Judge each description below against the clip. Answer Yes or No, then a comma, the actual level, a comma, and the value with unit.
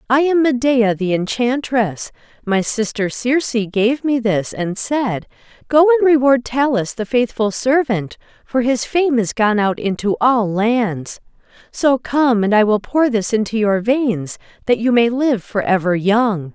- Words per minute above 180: No, average, 165 wpm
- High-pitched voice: Yes, high, 230 Hz